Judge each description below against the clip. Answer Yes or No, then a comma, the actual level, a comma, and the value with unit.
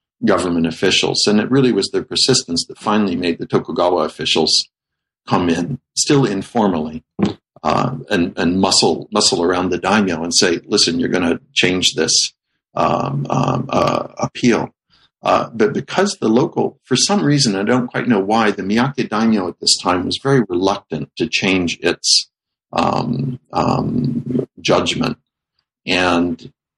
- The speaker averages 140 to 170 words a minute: Yes, average, 150 wpm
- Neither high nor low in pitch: No, very low, 95 Hz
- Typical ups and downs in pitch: No, wide, 6.5 semitones